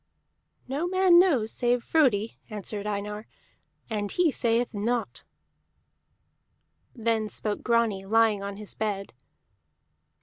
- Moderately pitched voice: No, high, 225 Hz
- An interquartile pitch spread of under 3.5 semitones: Yes, average, 2.9 semitones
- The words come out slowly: Yes, slow, 105 wpm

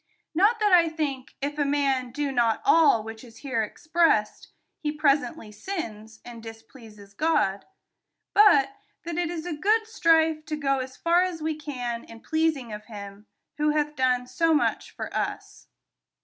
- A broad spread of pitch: Yes, wide, 5.7 semitones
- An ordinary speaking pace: Yes, average, 165 wpm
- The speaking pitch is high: Yes, very high, 290 Hz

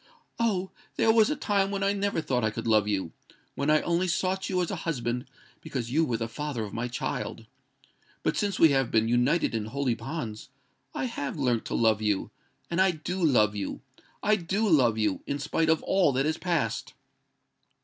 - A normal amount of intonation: No, wide, 8.0 semitones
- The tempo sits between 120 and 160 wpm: No, average, 185 wpm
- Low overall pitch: No, medium, 145 Hz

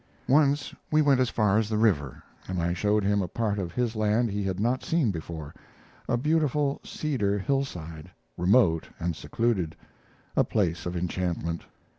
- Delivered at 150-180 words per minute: Yes, average, 165 wpm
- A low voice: Yes, low, 105 Hz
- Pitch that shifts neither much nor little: No, wide, 6.0 semitones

